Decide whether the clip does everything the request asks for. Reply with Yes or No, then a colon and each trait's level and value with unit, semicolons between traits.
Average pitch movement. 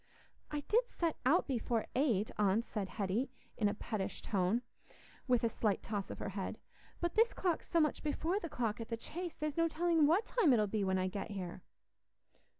No: wide, 8.0 semitones